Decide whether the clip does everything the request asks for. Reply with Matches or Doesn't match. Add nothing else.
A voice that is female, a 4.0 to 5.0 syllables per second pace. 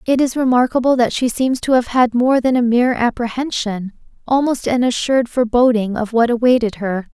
Doesn't match